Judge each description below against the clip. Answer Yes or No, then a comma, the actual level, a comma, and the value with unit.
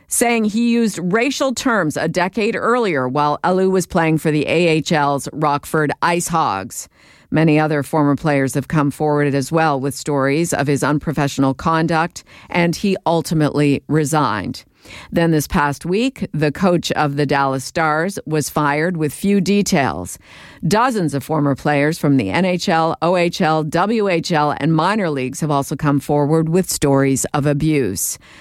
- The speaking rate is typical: Yes, average, 150 wpm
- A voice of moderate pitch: Yes, medium, 155 Hz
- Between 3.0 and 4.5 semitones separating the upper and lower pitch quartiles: Yes, average, 3.4 semitones